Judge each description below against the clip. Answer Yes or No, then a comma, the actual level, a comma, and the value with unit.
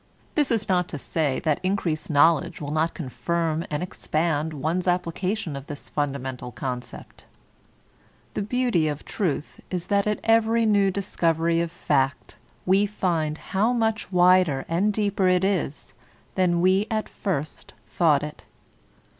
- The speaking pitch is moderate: Yes, medium, 175 Hz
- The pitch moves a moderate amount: Yes, average, 4.4 semitones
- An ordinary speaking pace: Yes, average, 150 wpm